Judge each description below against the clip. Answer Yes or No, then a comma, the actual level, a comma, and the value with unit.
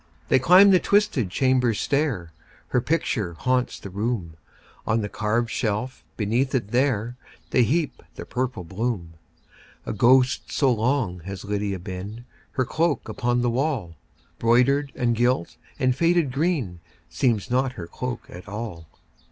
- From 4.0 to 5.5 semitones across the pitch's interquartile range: Yes, average, 4.4 semitones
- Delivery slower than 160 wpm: Yes, average, 145 wpm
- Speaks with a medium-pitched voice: No, low, 120 Hz